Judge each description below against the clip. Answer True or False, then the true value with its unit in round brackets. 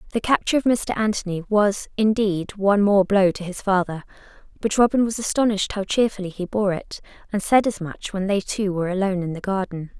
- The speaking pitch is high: True (200 Hz)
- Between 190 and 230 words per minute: True (205 wpm)